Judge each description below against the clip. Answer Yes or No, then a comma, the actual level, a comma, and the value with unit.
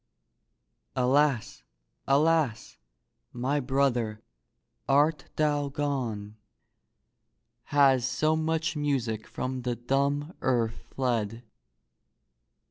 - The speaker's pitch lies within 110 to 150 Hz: Yes, low, 135 Hz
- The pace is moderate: No, slow, 75 wpm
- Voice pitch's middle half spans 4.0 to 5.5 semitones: No, average, 3.3 semitones